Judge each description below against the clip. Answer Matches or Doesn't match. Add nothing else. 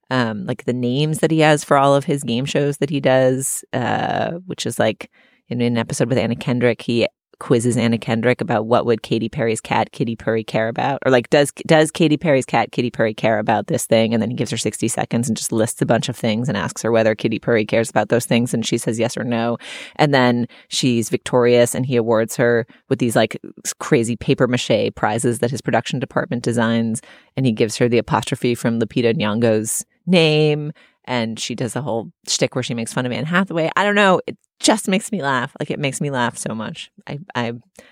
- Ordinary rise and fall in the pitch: Matches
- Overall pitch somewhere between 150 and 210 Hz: Doesn't match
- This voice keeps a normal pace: Doesn't match